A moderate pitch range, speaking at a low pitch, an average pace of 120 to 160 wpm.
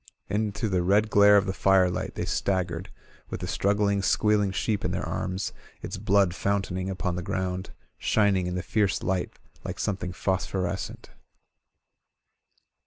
No: narrow, 1.7 semitones; very low, 95 Hz; average, 150 wpm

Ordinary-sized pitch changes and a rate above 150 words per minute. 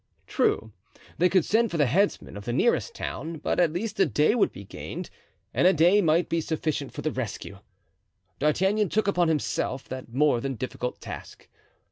No: wide, 6.4 semitones; average, 185 wpm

